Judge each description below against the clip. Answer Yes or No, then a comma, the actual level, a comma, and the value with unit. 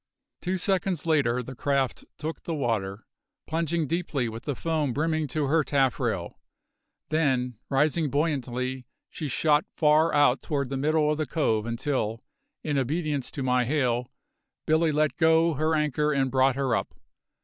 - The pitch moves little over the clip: No, average, 3.6 semitones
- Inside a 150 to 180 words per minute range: Yes, average, 155 wpm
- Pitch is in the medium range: Yes, medium, 145 Hz